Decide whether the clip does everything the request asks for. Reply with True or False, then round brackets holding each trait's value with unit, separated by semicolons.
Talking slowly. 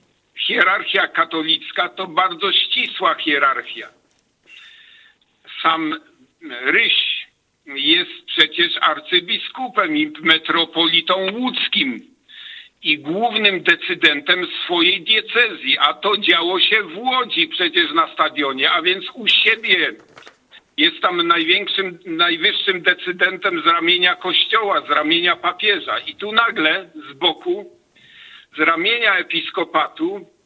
True (100 wpm)